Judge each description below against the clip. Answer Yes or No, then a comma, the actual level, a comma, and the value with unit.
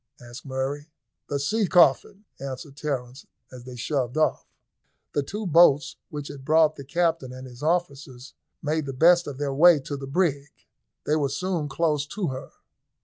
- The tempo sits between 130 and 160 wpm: No, average, 170 wpm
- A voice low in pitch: No, medium, 145 Hz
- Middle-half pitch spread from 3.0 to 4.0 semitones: Yes, average, 3.3 semitones